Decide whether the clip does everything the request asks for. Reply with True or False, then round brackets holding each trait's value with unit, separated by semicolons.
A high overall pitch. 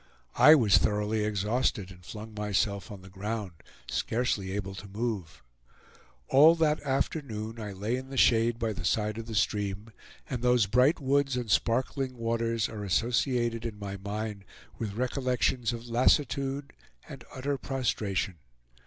False (115 Hz)